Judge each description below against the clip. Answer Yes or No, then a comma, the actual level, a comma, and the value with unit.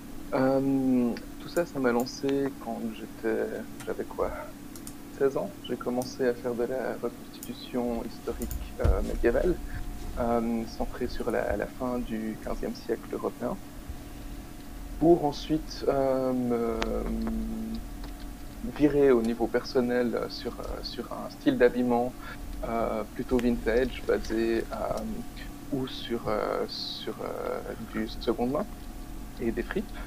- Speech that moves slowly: Yes, slow, 120 wpm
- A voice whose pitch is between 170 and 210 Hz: No, low, 125 Hz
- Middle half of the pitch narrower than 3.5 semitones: Yes, narrow, 2.4 semitones